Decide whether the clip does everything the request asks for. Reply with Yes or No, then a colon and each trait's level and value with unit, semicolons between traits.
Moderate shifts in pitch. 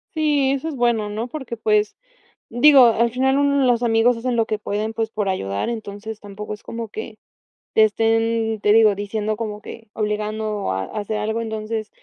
No: narrow, 1.9 semitones